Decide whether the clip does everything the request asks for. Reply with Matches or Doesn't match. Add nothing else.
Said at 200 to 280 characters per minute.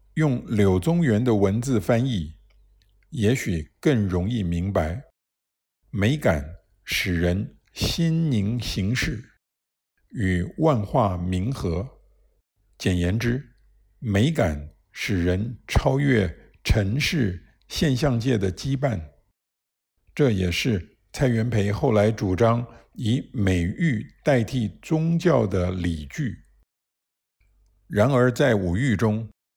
Doesn't match